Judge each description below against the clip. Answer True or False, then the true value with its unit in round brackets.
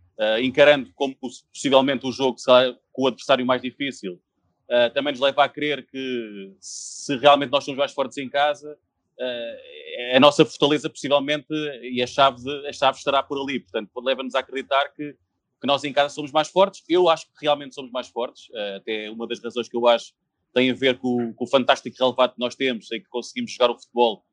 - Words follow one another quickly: True (210 wpm)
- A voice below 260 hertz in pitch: True (135 Hz)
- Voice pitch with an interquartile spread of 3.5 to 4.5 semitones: False (2.8 semitones)